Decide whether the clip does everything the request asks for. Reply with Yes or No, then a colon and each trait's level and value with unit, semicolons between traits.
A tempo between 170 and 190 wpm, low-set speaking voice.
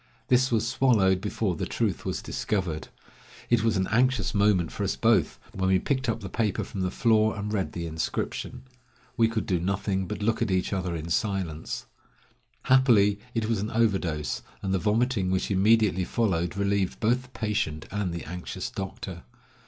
Yes: average, 180 wpm; low, 100 Hz